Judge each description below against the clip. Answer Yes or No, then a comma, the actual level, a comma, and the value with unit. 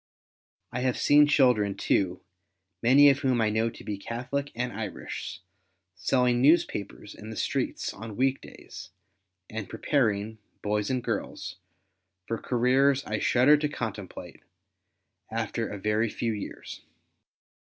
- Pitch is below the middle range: Yes, low, 115 Hz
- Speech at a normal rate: No, slow, 130 wpm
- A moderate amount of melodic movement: Yes, average, 3.7 semitones